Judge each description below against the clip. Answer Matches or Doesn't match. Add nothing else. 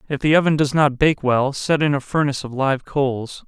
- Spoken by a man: Matches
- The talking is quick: Matches